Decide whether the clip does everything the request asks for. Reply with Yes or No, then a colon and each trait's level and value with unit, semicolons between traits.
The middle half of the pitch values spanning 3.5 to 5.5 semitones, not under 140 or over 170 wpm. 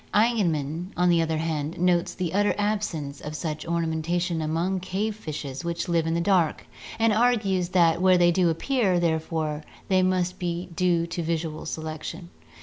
No: narrow, 2.5 semitones; average, 165 wpm